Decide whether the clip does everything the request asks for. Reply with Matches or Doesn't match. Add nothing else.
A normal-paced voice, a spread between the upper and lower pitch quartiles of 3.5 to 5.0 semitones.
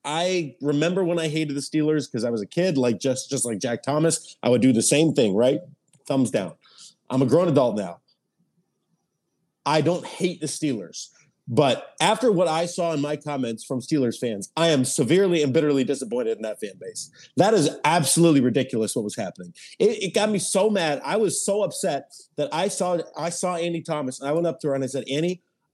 Doesn't match